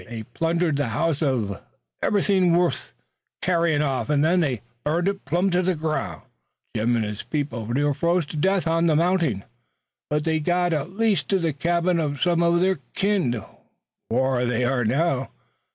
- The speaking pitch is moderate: Yes, medium, 160 Hz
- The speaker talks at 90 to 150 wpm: No, average, 175 wpm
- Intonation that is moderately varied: Yes, average, 4.8 semitones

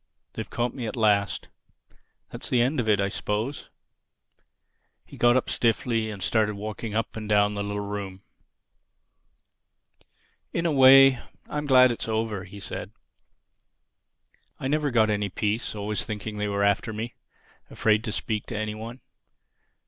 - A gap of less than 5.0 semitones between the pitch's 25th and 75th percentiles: Yes, average, 2.7 semitones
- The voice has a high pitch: No, low, 110 Hz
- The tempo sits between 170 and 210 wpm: No, average, 150 wpm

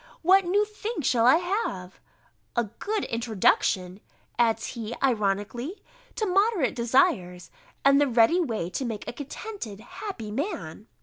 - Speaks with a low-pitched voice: No, high, 240 Hz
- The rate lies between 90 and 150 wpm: Yes, slow, 135 wpm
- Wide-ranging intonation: Yes, wide, 9.0 semitones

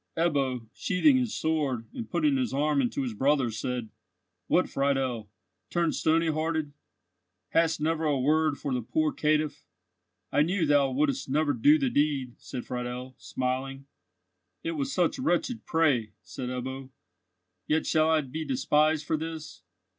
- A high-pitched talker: No, medium, 150 Hz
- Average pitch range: Yes, average, 3.5 semitones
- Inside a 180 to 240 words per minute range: No, average, 150 wpm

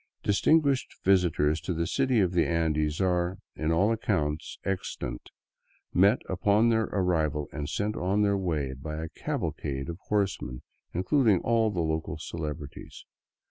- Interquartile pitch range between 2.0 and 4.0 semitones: No, average, 4.8 semitones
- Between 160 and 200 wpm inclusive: No, average, 140 wpm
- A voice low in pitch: Yes, very low, 90 Hz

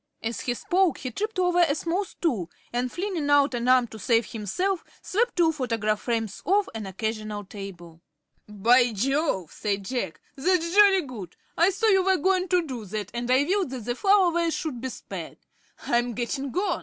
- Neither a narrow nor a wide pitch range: No, wide, 8.3 semitones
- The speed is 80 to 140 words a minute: No, average, 190 wpm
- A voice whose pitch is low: No, very high, 255 Hz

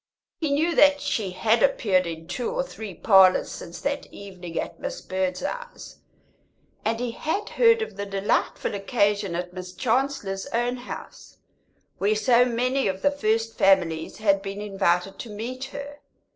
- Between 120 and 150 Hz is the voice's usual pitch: No, high, 215 Hz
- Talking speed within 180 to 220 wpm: No, average, 160 wpm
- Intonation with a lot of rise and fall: Yes, wide, 5.7 semitones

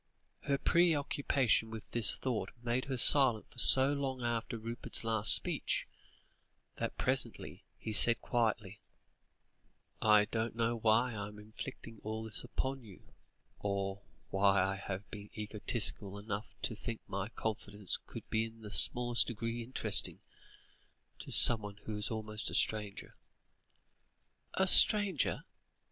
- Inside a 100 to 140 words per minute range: Yes, slow, 135 wpm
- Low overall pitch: Yes, low, 110 Hz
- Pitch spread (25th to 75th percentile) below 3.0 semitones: Yes, narrow, 2.5 semitones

